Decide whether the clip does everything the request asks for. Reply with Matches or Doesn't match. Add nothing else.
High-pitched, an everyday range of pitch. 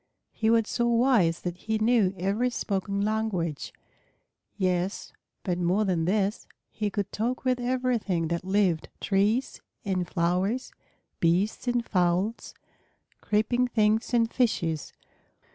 Matches